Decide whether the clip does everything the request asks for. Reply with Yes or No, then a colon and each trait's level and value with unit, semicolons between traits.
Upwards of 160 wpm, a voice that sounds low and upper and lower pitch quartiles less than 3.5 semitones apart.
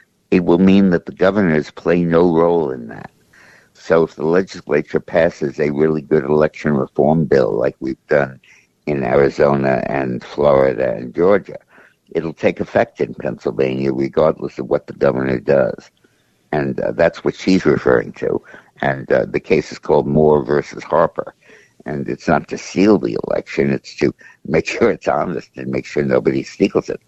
Yes: average, 170 wpm; very low, 70 Hz; average, 2.7 semitones